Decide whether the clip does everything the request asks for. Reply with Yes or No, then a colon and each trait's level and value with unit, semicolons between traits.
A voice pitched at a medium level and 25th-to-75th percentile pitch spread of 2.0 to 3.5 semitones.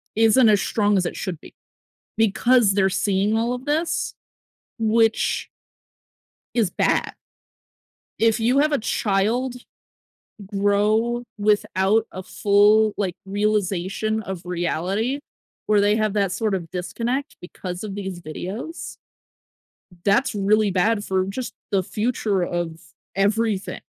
No: high, 205 Hz; average, 2.8 semitones